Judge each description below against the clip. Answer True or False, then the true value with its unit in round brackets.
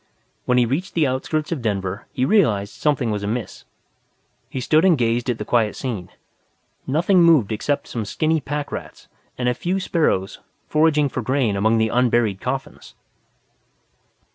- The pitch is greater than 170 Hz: False (125 Hz)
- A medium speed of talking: True (155 wpm)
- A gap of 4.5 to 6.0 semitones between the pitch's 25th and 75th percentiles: True (5.5 semitones)